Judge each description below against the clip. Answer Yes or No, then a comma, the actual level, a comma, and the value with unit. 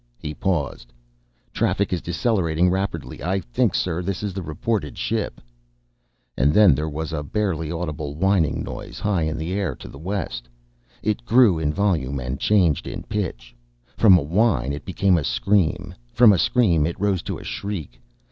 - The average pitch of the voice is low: Yes, very low, 85 Hz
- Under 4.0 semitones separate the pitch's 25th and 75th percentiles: No, average, 4.8 semitones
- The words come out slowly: No, average, 175 wpm